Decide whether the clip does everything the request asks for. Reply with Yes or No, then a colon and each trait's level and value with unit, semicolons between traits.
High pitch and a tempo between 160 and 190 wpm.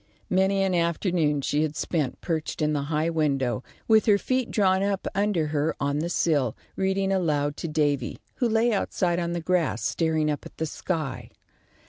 No: medium, 165 Hz; average, 180 wpm